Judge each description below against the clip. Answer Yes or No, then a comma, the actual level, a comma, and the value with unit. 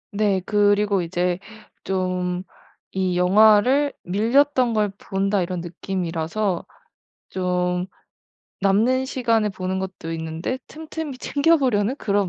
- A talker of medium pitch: No, high, 200 Hz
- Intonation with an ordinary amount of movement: Yes, average, 4.0 semitones